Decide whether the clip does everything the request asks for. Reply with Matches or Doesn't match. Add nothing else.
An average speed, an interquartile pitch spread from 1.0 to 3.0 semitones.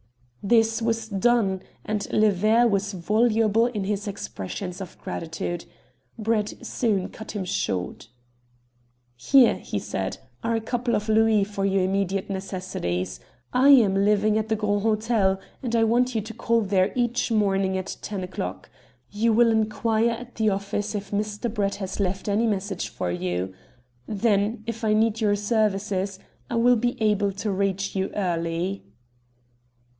Matches